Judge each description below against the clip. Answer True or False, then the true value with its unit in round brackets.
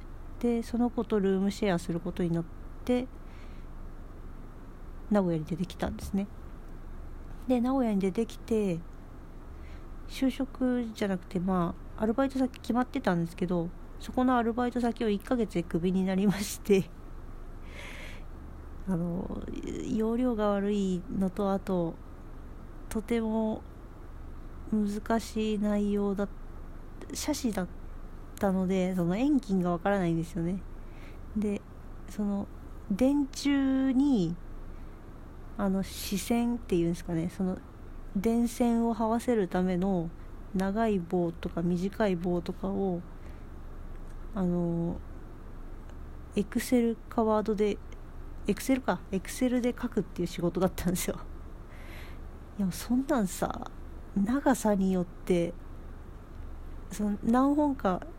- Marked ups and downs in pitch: False (5.0 semitones)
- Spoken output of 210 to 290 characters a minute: True (220 characters per minute)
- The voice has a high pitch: True (195 Hz)